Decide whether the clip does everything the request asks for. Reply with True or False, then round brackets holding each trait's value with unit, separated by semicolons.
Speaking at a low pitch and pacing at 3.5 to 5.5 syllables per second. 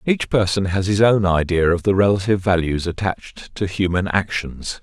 True (95 Hz; 5.1 syllables/s)